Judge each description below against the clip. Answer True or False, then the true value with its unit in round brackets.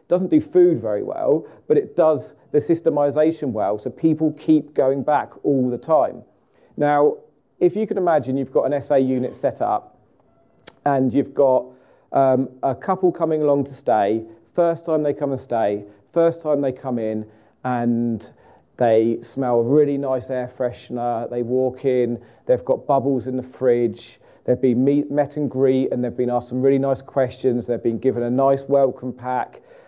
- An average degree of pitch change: True (3.1 semitones)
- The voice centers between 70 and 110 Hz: False (135 Hz)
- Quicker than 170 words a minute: True (180 wpm)